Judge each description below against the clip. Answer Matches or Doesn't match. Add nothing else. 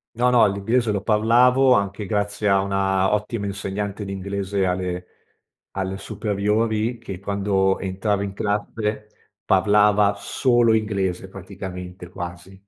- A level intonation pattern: Matches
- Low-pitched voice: Matches